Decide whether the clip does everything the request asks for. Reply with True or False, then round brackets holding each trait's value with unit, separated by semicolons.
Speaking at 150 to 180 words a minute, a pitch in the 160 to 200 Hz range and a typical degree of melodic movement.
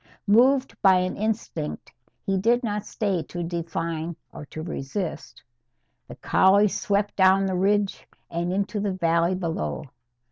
False (140 wpm; 190 Hz; 3.4 semitones)